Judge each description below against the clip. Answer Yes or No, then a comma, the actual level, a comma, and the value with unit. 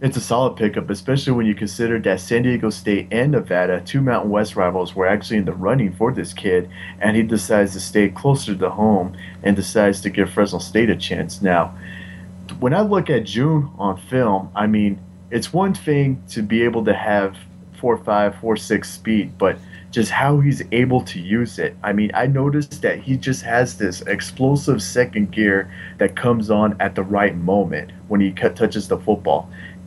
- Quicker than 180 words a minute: Yes, average, 195 wpm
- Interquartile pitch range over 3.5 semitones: Yes, average, 4.3 semitones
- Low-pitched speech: Yes, low, 105 Hz